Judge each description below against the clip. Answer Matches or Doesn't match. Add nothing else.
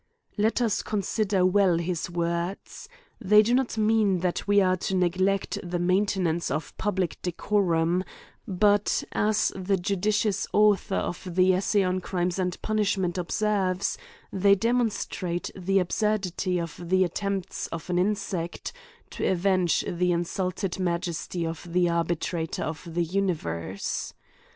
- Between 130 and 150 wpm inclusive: Matches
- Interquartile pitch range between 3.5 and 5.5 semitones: Doesn't match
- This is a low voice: Doesn't match